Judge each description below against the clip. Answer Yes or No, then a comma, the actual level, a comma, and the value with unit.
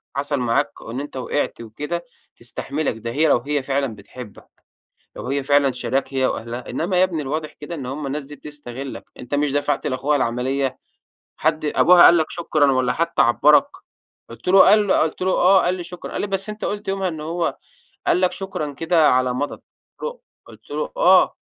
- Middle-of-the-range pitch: Yes, medium, 145 Hz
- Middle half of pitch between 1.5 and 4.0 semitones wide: No, average, 4.8 semitones